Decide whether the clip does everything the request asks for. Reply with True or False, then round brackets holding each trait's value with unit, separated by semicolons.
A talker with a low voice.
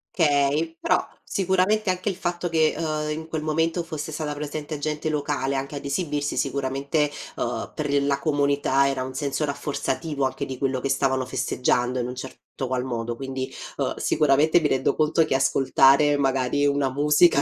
False (145 Hz)